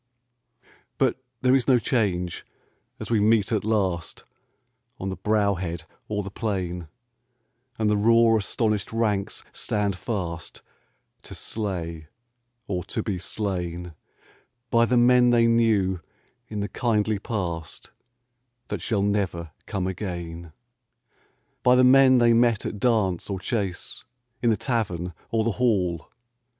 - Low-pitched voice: Yes, low, 105 Hz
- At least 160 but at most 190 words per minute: No, slow, 135 wpm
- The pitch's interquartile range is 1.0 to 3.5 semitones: No, average, 4.1 semitones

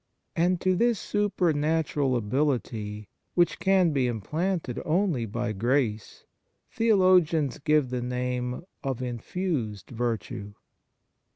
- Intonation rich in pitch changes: Yes, wide, 6.5 semitones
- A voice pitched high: No, medium, 140 Hz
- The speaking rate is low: Yes, slow, 105 wpm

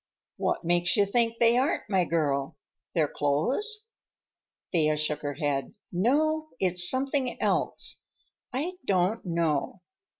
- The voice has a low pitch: No, medium, 185 Hz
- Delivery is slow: Yes, slow, 125 wpm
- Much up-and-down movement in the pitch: Yes, wide, 8.8 semitones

